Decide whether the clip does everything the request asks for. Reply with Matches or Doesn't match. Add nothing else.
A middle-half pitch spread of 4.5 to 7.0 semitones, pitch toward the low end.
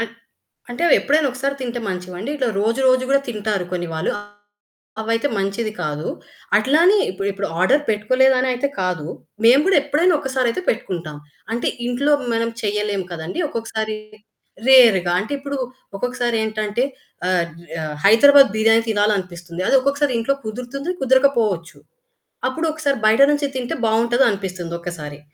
Doesn't match